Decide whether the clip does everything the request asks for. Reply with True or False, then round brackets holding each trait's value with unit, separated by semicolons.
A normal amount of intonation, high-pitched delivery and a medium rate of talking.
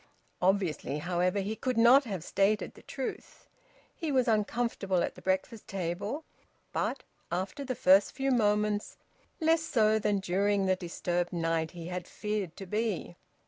True (4.1 semitones; 200 Hz; 150 wpm)